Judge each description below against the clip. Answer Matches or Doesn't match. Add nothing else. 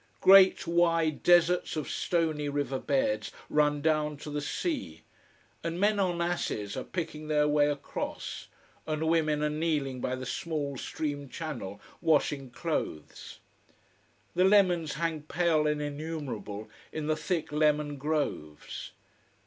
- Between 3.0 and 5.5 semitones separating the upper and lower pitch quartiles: Doesn't match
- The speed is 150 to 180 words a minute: Doesn't match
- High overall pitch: Doesn't match